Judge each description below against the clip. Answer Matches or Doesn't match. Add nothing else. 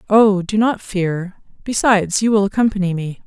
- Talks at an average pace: Matches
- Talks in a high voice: Matches